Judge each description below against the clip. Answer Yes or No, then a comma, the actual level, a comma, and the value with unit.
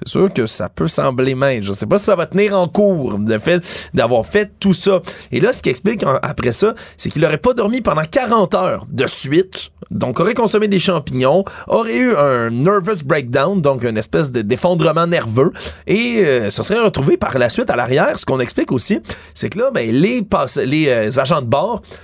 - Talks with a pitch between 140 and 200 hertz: Yes, medium, 185 Hz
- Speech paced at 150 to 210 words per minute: No, fast, 220 wpm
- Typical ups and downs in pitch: No, wide, 6.9 semitones